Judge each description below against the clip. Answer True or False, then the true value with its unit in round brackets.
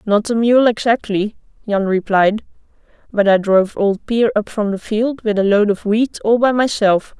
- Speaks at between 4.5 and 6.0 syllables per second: True (4.7 syllables/s)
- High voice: True (215 Hz)